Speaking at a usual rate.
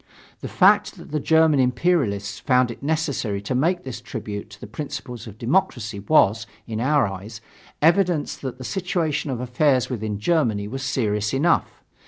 Yes: average, 165 wpm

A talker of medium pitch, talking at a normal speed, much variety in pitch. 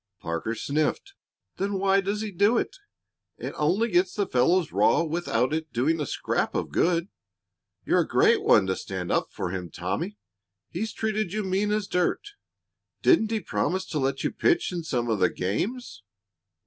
Yes: medium, 175 Hz; average, 175 wpm; wide, 8.9 semitones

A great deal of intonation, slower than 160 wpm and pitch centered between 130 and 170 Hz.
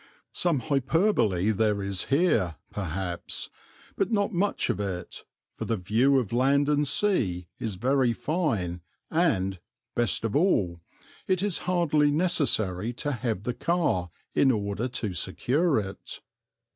No: wide, 8.1 semitones; slow, 135 wpm; low, 120 Hz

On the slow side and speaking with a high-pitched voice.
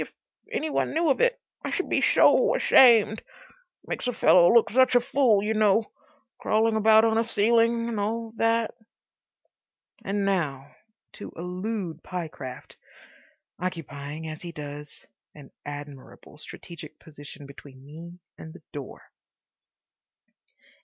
Yes: slow, 130 wpm; high, 195 Hz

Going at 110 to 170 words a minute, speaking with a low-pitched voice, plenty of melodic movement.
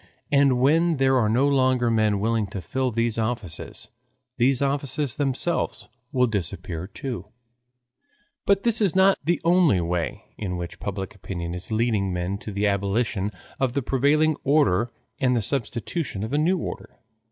Yes: average, 160 wpm; low, 120 Hz; wide, 5.9 semitones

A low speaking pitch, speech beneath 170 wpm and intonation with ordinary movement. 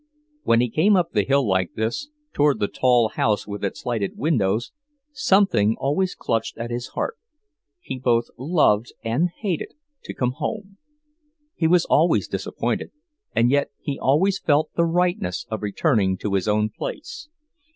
No: low, 125 Hz; average, 160 wpm; wide, 7.7 semitones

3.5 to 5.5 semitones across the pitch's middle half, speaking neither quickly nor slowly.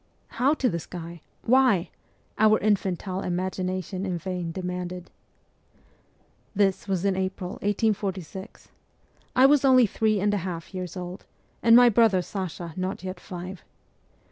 No: average, 2.7 semitones; average, 145 wpm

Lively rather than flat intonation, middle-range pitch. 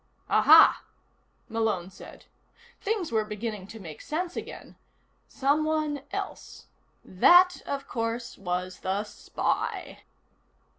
No: wide, 7.5 semitones; high, 230 Hz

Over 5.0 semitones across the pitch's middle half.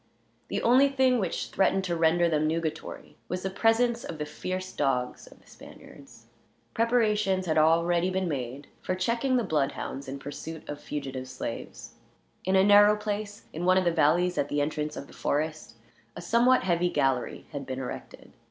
Yes: wide, 5.5 semitones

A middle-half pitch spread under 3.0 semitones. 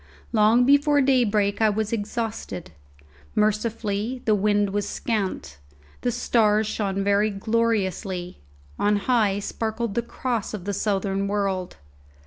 Yes: narrow, 2.5 semitones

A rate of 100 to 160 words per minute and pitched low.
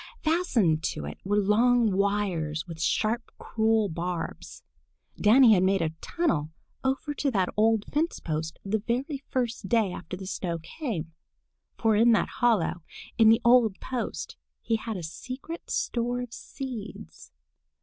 No: average, 150 wpm; high, 220 Hz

